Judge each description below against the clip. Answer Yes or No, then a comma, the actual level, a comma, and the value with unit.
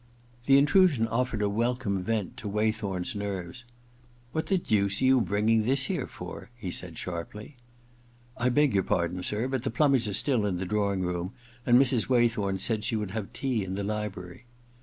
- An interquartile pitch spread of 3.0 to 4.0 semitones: Yes, average, 3.7 semitones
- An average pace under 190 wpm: No, average, 200 wpm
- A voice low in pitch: Yes, low, 110 Hz